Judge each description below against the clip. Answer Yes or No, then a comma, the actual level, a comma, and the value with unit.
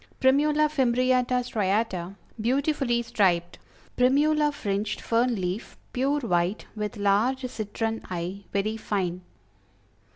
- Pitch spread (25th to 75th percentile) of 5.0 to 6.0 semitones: No, average, 4.6 semitones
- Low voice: No, high, 230 Hz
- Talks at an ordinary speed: No, slow, 100 wpm